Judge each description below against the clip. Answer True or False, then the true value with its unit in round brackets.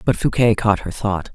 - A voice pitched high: False (105 Hz)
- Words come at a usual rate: False (225 wpm)